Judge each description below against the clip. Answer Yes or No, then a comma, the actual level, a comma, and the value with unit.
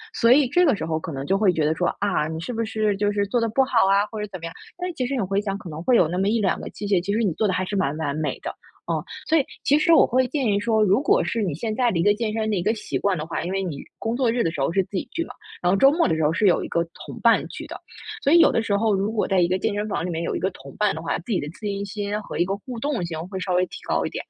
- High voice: Yes, high, 200 Hz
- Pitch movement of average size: Yes, average, 4.3 semitones